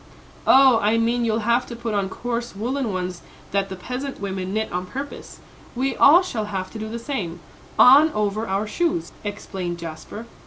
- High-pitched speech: Yes, high, 220 Hz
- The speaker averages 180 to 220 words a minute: Yes, average, 185 wpm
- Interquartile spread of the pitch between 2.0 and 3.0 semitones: No, average, 4.3 semitones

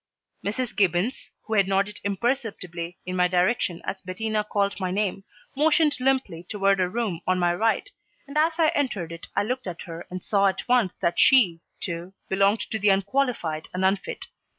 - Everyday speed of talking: Yes, average, 180 wpm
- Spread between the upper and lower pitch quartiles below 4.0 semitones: No, average, 4.7 semitones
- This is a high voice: Yes, high, 200 Hz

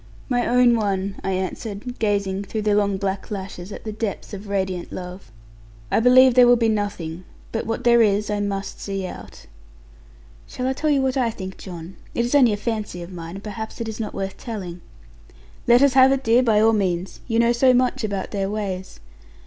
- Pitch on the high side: Yes, high, 210 Hz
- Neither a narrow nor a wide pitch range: Yes, average, 3.6 semitones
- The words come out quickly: Yes, fast, 210 wpm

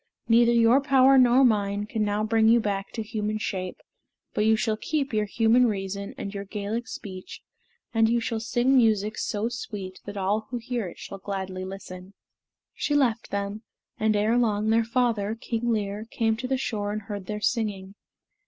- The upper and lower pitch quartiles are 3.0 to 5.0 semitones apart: No, narrow, 2.6 semitones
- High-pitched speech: Yes, high, 215 Hz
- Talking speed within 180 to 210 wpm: Yes, average, 185 wpm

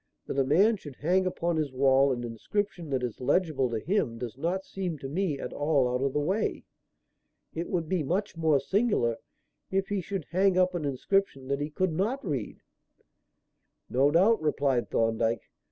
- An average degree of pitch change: No, wide, 5.9 semitones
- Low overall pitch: No, medium, 155 Hz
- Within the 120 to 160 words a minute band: No, average, 185 wpm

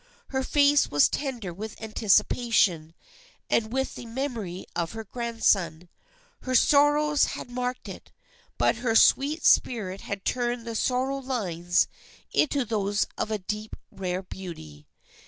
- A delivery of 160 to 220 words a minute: No, average, 140 wpm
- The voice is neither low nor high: No, high, 225 Hz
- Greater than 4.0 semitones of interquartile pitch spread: Yes, average, 5.2 semitones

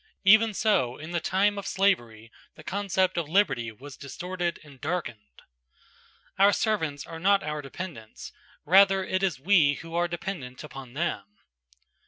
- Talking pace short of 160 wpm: Yes, average, 150 wpm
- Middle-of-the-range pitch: Yes, medium, 170 Hz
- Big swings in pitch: Yes, wide, 5.9 semitones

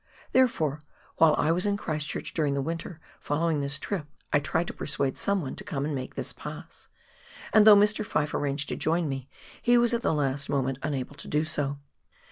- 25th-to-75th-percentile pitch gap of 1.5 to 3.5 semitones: No, average, 4.2 semitones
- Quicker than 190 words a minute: Yes, fast, 205 wpm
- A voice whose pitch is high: No, medium, 155 Hz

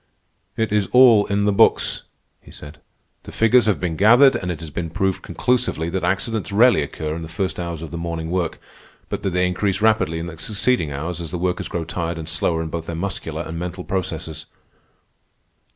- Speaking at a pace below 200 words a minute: No, fast, 205 wpm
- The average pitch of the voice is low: Yes, very low, 90 Hz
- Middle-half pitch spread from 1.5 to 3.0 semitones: No, average, 3.7 semitones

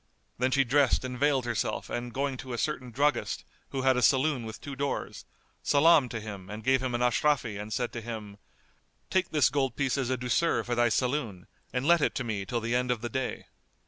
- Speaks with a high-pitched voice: No, low, 125 Hz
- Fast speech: Yes, fast, 225 wpm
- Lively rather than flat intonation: No, average, 2.9 semitones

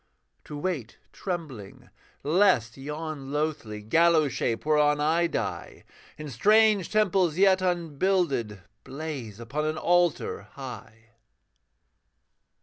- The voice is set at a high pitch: No, medium, 150 Hz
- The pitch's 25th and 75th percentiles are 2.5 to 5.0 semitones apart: No, wide, 5.5 semitones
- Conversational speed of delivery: No, slow, 100 wpm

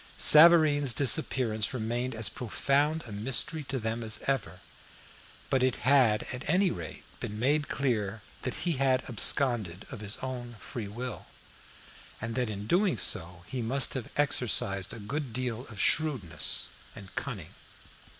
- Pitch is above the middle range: No, low, 125 Hz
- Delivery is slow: No, average, 150 wpm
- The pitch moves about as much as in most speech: Yes, average, 4.2 semitones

